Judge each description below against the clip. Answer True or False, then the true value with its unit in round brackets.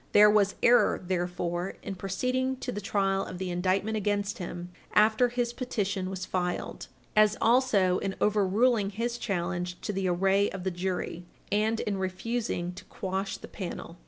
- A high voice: True (195 Hz)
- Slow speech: False (160 wpm)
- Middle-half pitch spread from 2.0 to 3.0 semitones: True (2.6 semitones)